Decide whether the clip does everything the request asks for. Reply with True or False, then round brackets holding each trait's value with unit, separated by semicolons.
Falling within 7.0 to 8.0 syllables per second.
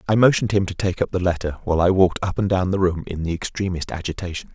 True (7.1 syllables/s)